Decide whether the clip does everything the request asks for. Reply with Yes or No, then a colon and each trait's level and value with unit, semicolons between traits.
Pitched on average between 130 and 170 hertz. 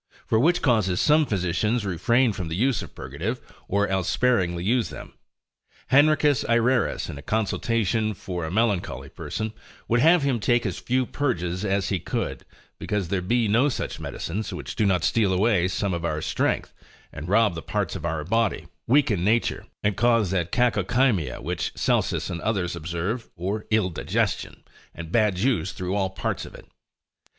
No: low, 105 Hz